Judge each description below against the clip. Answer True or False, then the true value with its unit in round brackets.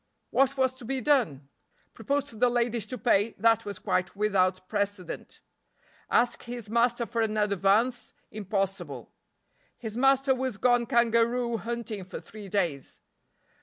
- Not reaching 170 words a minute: True (140 wpm)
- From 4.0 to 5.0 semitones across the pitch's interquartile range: False (3.4 semitones)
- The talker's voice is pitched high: True (230 Hz)